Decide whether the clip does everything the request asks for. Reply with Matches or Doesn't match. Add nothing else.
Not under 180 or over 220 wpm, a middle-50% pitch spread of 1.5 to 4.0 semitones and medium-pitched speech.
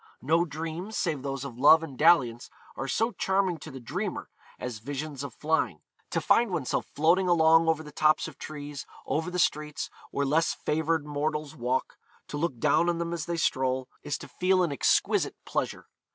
Matches